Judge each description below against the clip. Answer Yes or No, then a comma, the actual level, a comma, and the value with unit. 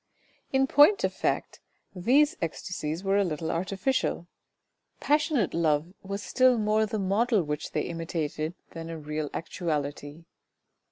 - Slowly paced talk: Yes, slow, 130 wpm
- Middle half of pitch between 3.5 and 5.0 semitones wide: No, wide, 5.4 semitones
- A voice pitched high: No, medium, 180 Hz